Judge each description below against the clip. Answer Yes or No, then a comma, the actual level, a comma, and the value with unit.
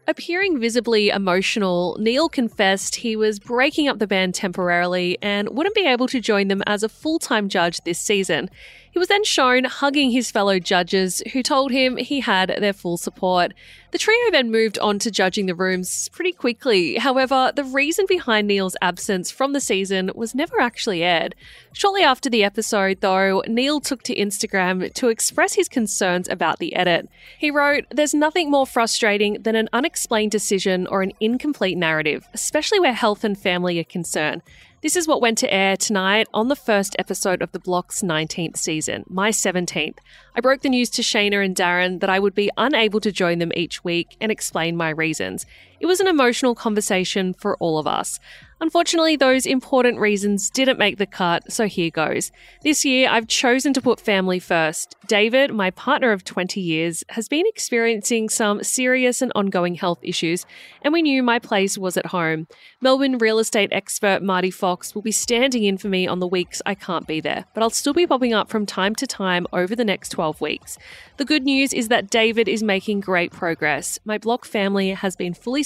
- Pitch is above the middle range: Yes, high, 215 Hz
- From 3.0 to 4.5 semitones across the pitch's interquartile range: No, wide, 5.6 semitones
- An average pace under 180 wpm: No, average, 195 wpm